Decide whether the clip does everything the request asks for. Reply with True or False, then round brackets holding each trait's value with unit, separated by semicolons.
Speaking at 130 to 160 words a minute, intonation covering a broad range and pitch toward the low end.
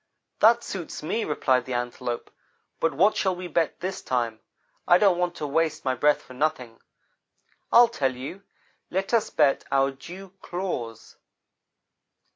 False (150 wpm; 6.2 semitones; 155 Hz)